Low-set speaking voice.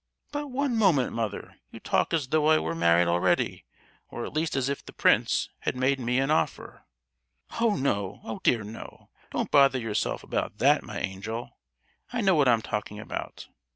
Yes: low, 130 Hz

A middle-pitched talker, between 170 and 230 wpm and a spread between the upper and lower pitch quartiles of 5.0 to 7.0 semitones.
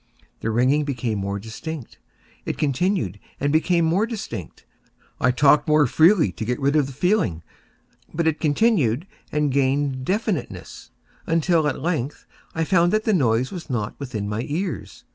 No: medium, 145 Hz; average, 150 wpm; wide, 5.4 semitones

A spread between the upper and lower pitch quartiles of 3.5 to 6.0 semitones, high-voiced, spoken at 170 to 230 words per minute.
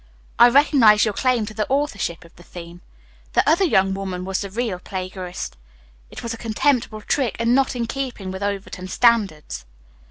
Yes: average, 4.5 semitones; high, 215 Hz; average, 180 wpm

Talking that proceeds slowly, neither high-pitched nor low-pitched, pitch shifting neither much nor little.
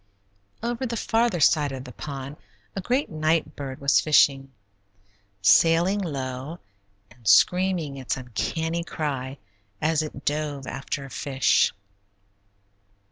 Yes: slow, 120 wpm; medium, 150 Hz; average, 3.8 semitones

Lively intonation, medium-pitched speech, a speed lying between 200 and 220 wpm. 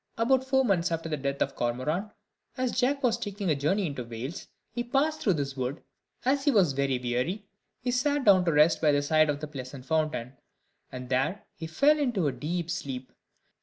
Yes: wide, 9.0 semitones; medium, 160 Hz; fast, 205 wpm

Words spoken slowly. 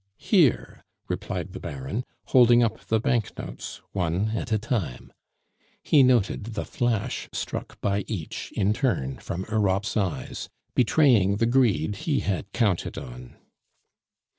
Yes: slow, 130 wpm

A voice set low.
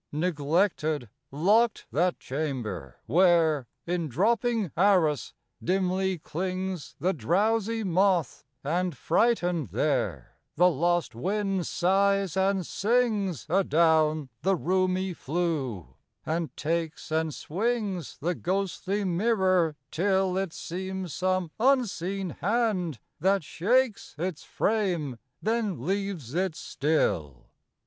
No: medium, 180 Hz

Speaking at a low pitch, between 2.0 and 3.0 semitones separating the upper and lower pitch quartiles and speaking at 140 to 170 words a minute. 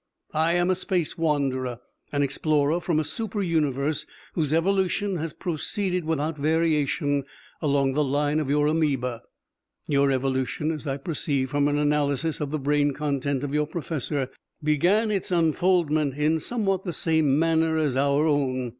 No: medium, 150 Hz; narrow, 2.6 semitones; average, 155 wpm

